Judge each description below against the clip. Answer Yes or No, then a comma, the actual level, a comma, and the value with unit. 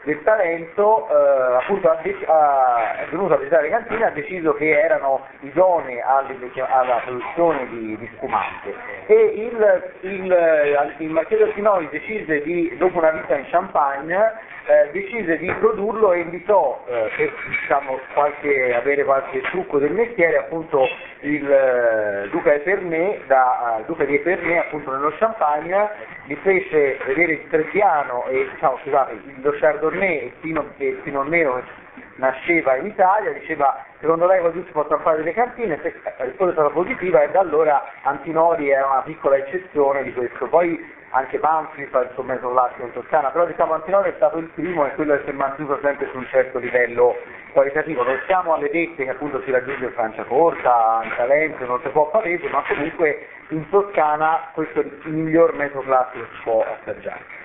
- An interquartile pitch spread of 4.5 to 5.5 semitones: Yes, average, 5.2 semitones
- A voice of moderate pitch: Yes, medium, 155 Hz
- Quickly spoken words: Yes, fast, 175 wpm